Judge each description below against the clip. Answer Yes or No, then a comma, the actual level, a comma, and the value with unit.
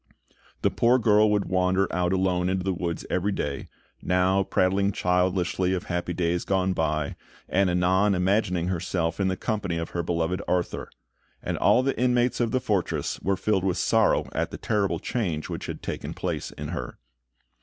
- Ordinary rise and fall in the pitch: No, narrow, 2.1 semitones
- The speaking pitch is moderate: No, very low, 95 Hz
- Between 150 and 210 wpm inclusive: Yes, average, 175 wpm